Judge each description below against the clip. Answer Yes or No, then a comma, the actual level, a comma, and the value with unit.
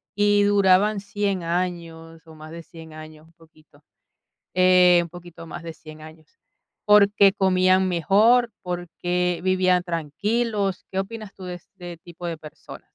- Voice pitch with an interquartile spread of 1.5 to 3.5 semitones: Yes, average, 3.0 semitones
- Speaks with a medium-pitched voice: Yes, medium, 180 Hz